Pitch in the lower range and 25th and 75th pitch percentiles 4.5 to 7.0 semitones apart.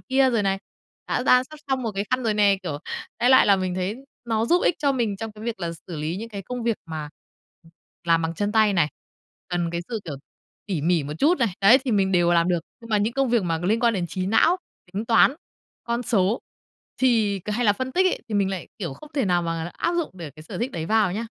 No: high, 205 Hz; average, 5.0 semitones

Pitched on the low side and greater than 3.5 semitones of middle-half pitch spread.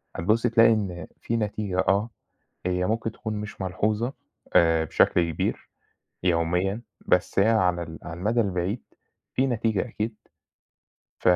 Yes: low, 100 Hz; average, 4.0 semitones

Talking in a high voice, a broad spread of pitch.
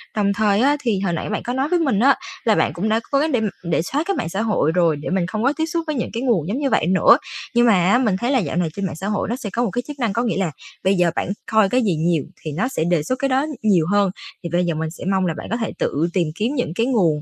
Yes: high, 205 Hz; wide, 5.9 semitones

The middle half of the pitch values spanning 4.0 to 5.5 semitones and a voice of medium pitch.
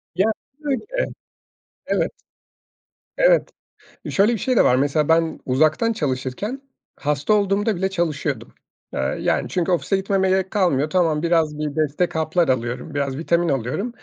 Yes: average, 5.1 semitones; medium, 165 Hz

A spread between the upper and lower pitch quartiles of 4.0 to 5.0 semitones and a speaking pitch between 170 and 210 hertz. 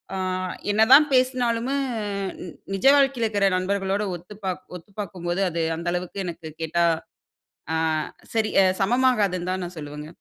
Yes: average, 4.6 semitones; high, 195 Hz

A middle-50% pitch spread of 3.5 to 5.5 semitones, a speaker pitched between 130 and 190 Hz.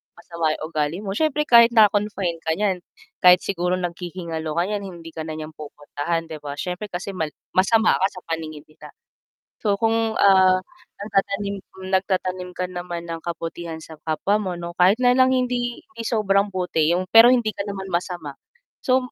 Yes: average, 3.9 semitones; medium, 185 Hz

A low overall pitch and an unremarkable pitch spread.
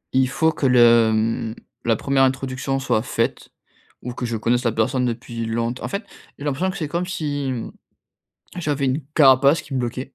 Yes: low, 130 Hz; average, 3.4 semitones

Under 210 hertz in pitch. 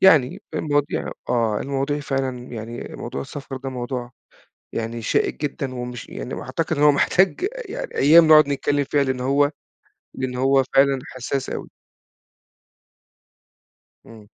Yes: low, 135 Hz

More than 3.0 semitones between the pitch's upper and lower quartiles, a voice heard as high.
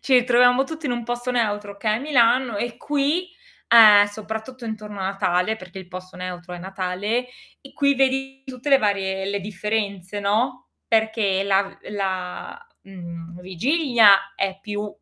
Yes: average, 4.4 semitones; high, 210 Hz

